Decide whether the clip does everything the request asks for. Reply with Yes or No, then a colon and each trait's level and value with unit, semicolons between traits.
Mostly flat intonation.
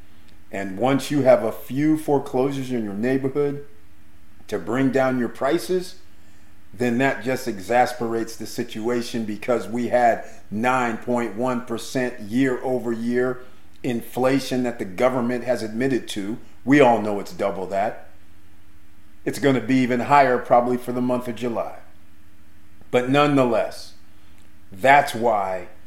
No: average, 4.5 semitones